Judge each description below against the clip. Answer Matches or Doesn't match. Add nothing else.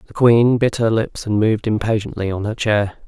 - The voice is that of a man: Matches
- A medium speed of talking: Doesn't match